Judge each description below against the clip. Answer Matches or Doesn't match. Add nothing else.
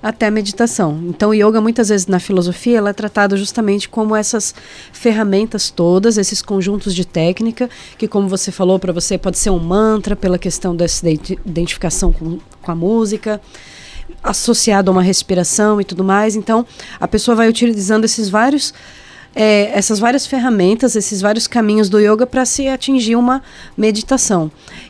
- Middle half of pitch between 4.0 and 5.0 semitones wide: Doesn't match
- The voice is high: Matches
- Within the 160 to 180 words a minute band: Matches